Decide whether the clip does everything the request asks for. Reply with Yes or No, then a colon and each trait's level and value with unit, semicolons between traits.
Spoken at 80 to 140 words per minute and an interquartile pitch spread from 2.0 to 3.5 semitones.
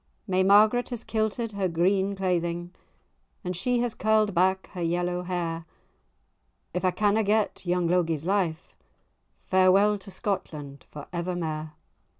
Yes: slow, 135 wpm; average, 2.9 semitones